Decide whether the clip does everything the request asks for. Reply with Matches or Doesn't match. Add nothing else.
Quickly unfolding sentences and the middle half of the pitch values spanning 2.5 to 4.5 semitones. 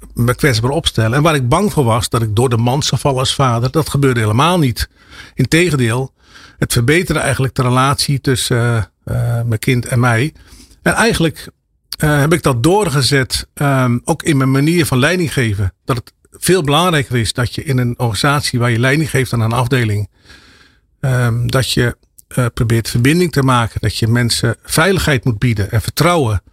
Doesn't match